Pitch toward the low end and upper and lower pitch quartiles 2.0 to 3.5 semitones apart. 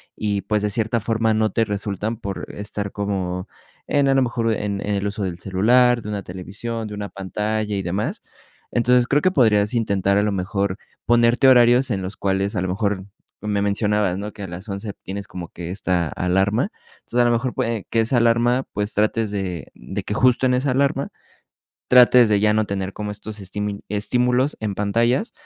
Yes: low, 105 Hz; average, 3.1 semitones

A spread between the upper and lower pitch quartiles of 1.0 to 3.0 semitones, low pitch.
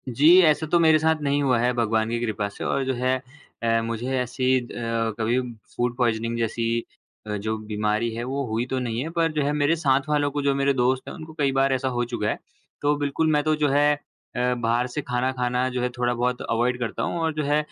No: average, 3.5 semitones; low, 125 Hz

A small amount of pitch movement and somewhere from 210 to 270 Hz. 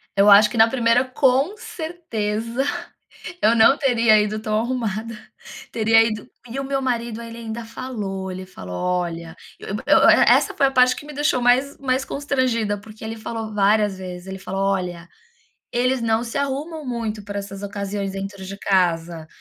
No: average, 4.2 semitones; high, 220 Hz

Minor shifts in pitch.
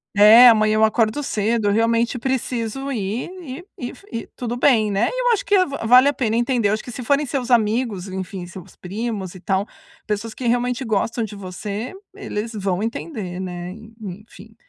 No: average, 3.4 semitones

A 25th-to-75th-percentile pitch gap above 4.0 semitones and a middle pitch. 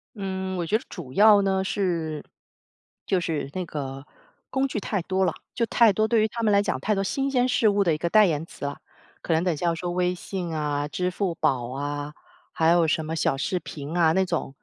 Yes: average, 4.4 semitones; medium, 175 Hz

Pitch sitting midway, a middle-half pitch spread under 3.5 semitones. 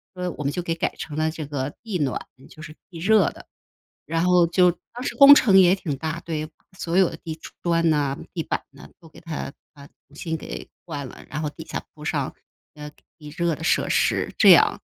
Yes: medium, 160 Hz; average, 2.9 semitones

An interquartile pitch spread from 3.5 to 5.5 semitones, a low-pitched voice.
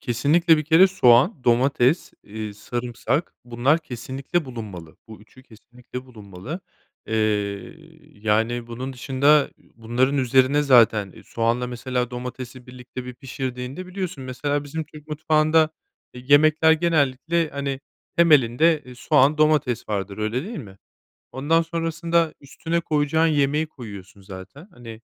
Yes: average, 4.3 semitones; low, 130 Hz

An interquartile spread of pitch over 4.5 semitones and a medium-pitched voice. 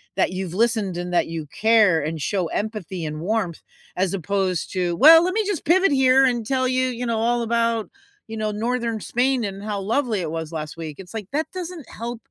No: wide, 5.4 semitones; high, 220 Hz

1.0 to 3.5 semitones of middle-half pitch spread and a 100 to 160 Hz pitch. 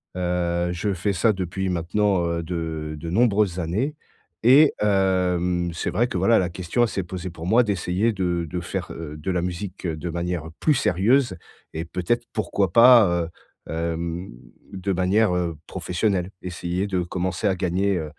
No: narrow, 2.6 semitones; very low, 90 Hz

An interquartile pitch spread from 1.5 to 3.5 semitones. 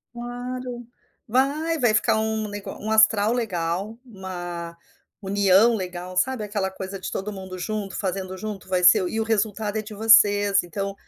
Yes: average, 2.9 semitones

